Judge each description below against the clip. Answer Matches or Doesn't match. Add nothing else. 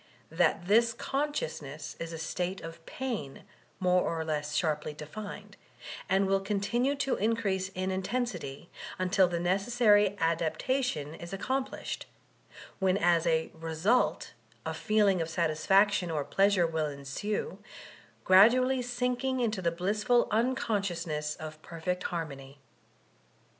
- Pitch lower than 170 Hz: Doesn't match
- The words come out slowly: Matches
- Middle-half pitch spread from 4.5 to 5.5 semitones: Matches